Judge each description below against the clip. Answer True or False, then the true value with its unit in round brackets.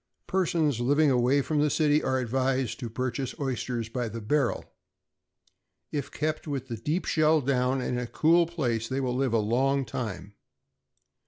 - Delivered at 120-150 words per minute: False (175 wpm)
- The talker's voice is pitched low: True (130 Hz)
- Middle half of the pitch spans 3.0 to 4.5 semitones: True (3.6 semitones)